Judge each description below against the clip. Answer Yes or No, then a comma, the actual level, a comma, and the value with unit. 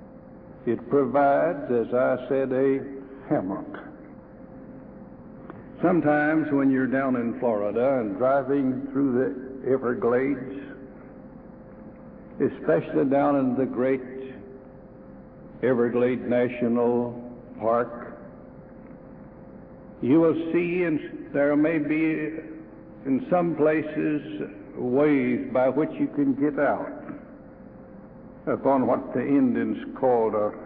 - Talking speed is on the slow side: Yes, slow, 95 wpm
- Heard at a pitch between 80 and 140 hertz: Yes, low, 135 Hz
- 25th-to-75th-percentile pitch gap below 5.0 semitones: Yes, average, 3.8 semitones